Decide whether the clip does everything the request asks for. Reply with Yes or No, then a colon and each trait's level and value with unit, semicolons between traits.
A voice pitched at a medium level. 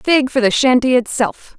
No: very high, 255 Hz